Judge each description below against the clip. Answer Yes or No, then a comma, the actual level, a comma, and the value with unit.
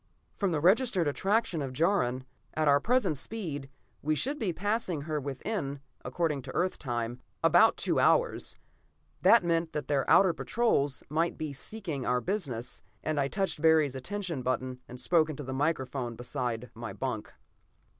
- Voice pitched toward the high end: No, medium, 150 Hz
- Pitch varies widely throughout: Yes, wide, 5.9 semitones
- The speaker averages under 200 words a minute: Yes, average, 160 wpm